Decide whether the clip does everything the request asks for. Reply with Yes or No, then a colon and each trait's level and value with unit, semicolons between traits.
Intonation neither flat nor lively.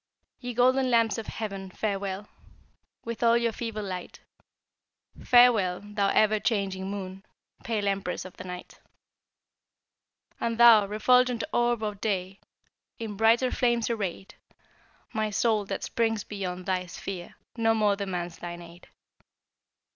Yes: average, 3.2 semitones